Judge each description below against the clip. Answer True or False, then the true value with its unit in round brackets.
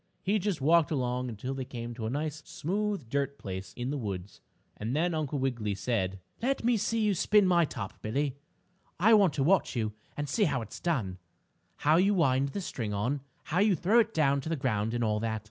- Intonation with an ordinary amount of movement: False (7.2 semitones)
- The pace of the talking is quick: True (215 wpm)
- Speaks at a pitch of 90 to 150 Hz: True (140 Hz)